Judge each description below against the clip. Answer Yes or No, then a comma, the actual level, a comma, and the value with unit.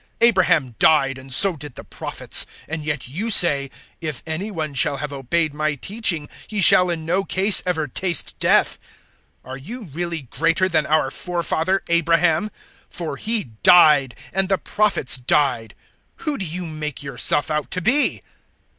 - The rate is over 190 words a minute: No, average, 165 wpm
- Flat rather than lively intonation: No, average, 4.3 semitones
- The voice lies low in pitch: No, medium, 160 Hz